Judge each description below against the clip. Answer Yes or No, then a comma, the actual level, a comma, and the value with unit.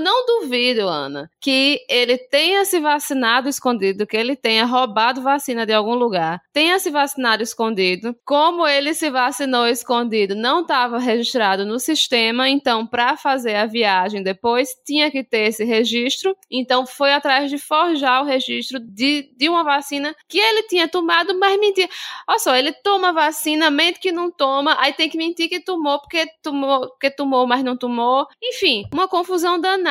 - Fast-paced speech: No, average, 170 wpm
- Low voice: No, very high, 275 Hz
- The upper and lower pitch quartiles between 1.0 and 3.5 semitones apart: No, average, 5.0 semitones